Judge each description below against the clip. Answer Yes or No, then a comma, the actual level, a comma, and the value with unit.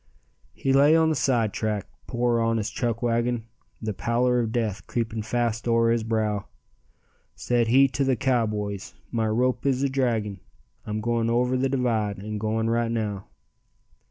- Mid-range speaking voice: No, low, 115 Hz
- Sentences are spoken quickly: No, average, 155 wpm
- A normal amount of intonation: No, narrow, 2.2 semitones